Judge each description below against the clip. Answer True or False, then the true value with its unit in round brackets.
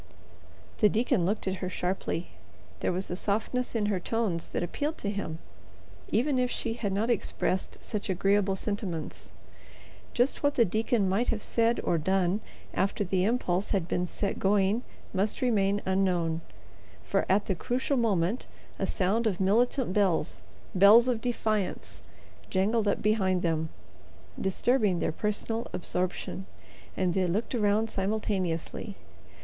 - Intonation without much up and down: False (3.4 semitones)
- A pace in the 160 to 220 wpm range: False (145 wpm)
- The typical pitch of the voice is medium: False (200 Hz)